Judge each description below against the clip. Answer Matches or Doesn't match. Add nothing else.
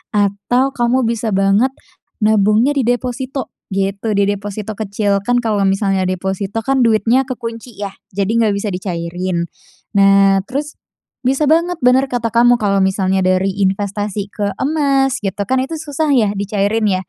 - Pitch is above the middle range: Matches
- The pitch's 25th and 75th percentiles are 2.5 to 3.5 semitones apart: Doesn't match